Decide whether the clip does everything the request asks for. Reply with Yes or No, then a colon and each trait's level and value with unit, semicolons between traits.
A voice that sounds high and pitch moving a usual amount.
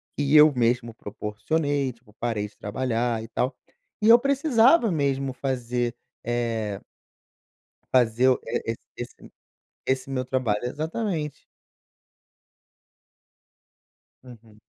No: low, 125 Hz; average, 4.0 semitones